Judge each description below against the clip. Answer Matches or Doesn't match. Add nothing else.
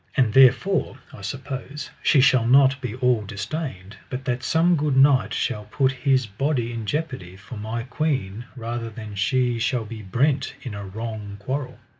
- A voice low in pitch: Matches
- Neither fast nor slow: Matches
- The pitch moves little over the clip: Doesn't match